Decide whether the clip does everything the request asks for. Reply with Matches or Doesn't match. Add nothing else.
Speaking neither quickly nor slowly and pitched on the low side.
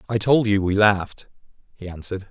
Matches